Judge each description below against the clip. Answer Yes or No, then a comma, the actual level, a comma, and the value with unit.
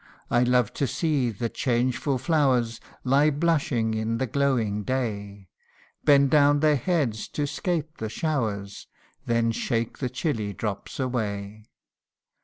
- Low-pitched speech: Yes, low, 125 Hz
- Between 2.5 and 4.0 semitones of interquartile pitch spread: No, average, 4.5 semitones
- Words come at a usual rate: No, slow, 130 wpm